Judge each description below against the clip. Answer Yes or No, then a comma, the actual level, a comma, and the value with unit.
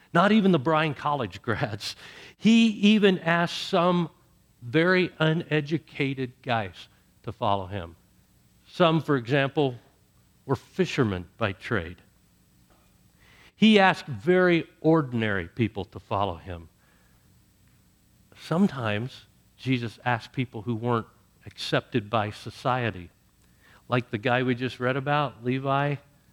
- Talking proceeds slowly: Yes, slow, 110 wpm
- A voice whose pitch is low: Yes, low, 125 Hz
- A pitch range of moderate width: No, wide, 6.9 semitones